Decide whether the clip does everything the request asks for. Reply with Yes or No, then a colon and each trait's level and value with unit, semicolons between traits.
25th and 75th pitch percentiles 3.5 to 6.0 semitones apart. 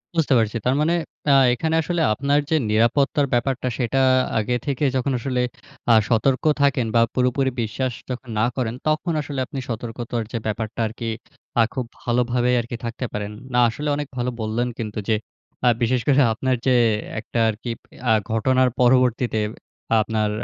No: average, 2.8 semitones